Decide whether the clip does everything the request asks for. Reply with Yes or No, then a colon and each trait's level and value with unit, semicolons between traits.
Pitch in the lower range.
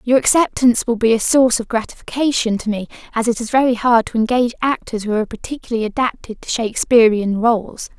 No: high, 235 Hz